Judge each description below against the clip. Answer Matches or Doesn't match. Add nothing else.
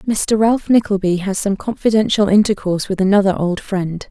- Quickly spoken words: Doesn't match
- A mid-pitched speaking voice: Doesn't match